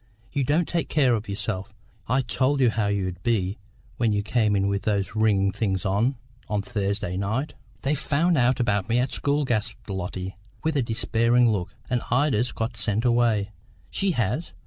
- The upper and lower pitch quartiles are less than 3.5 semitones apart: No, average, 4.0 semitones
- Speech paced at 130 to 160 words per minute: No, average, 190 wpm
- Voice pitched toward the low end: Yes, low, 115 Hz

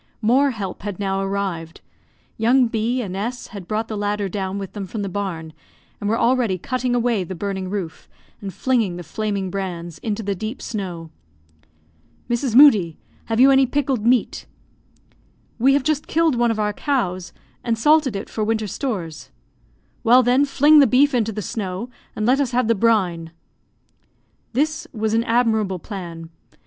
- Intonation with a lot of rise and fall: No, average, 4.3 semitones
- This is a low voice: No, high, 215 Hz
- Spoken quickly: No, average, 170 wpm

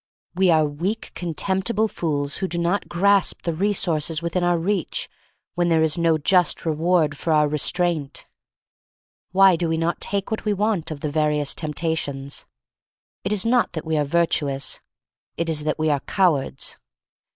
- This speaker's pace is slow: No, average, 170 wpm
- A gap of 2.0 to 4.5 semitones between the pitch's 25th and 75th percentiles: Yes, average, 3.3 semitones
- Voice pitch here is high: No, medium, 165 Hz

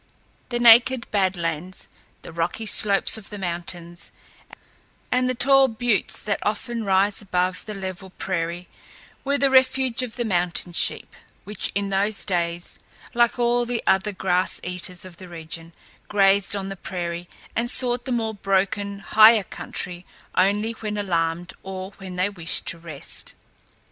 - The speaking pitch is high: Yes, high, 195 Hz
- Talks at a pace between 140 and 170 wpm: Yes, average, 155 wpm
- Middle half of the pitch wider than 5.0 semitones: No, average, 4.1 semitones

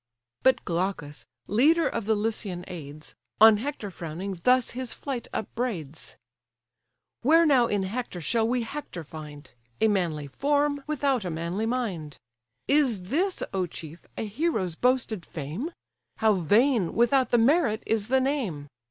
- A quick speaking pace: No, average, 145 wpm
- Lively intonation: Yes, wide, 6.8 semitones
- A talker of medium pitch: No, high, 220 Hz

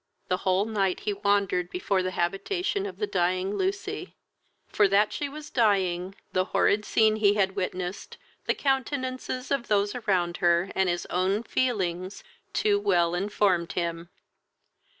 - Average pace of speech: Yes, average, 150 wpm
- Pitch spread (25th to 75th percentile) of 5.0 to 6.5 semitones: No, average, 3.3 semitones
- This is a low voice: No, high, 200 Hz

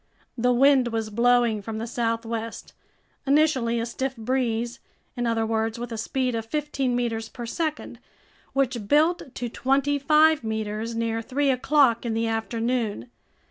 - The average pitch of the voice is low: No, high, 235 Hz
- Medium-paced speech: Yes, average, 150 wpm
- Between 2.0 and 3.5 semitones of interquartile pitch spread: Yes, average, 2.9 semitones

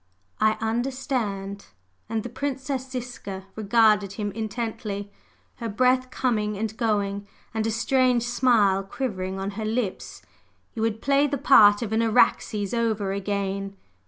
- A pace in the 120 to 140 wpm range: Yes, slow, 135 wpm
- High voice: Yes, high, 220 Hz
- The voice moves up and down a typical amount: Yes, average, 3.4 semitones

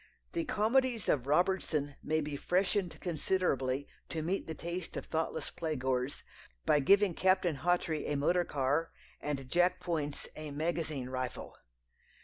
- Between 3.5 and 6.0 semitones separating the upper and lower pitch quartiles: Yes, average, 4.0 semitones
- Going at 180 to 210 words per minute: No, average, 140 wpm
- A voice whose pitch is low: No, medium, 160 Hz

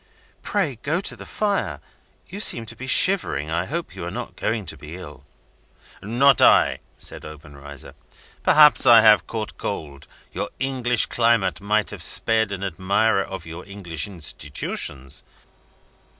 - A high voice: No, low, 100 Hz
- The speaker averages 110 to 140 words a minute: No, average, 150 wpm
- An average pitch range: No, wide, 6.8 semitones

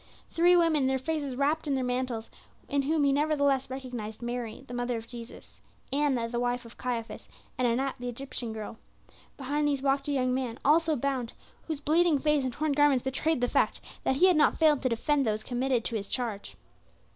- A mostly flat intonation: No, average, 3.2 semitones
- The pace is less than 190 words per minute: No, average, 200 wpm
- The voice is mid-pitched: No, very high, 265 Hz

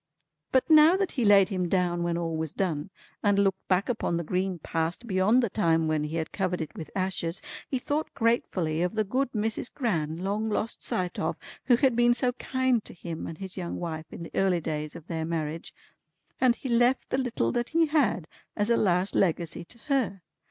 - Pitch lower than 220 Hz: Yes, high, 190 Hz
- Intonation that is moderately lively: No, wide, 6.1 semitones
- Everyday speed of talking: No, fast, 210 wpm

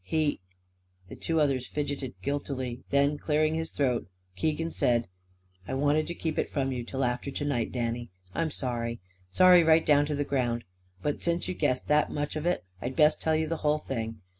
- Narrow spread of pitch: No, average, 4.0 semitones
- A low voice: No, medium, 145 Hz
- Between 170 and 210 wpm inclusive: Yes, average, 200 wpm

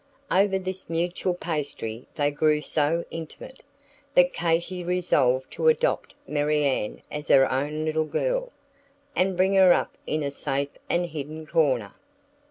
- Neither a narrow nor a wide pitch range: Yes, average, 3.8 semitones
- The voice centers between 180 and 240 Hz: No, medium, 160 Hz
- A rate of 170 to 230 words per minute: No, average, 140 wpm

